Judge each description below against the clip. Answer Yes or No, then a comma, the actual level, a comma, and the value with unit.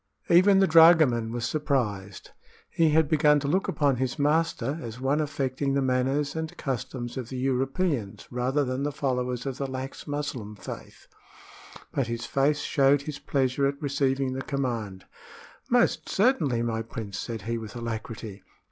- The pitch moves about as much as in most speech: Yes, average, 3.5 semitones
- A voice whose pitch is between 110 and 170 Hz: Yes, low, 135 Hz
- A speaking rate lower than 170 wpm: Yes, average, 160 wpm